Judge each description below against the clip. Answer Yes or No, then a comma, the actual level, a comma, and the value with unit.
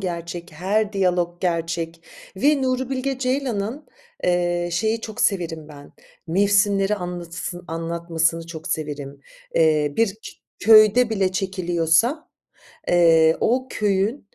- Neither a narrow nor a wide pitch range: Yes, average, 4.5 semitones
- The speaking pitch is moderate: Yes, medium, 180 Hz